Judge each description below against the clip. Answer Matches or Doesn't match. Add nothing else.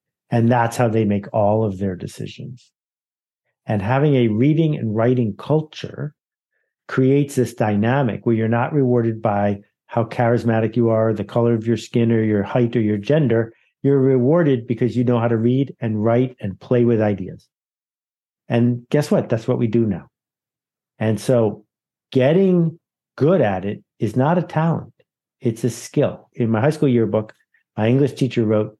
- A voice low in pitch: Matches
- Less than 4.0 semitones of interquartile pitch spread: Matches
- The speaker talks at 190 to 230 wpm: Doesn't match